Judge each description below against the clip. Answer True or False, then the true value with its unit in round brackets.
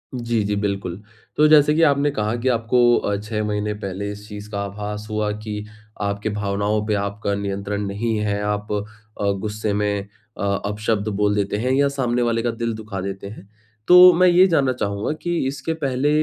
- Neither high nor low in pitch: False (105 Hz)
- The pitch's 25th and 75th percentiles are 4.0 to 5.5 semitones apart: False (2.8 semitones)